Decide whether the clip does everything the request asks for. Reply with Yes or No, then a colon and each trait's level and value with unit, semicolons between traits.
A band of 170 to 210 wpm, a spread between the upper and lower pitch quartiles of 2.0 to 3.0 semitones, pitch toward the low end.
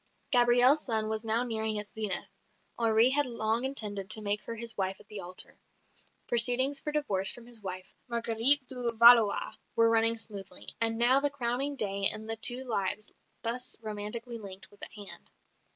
No: average, 175 wpm; narrow, 2.6 semitones; high, 230 Hz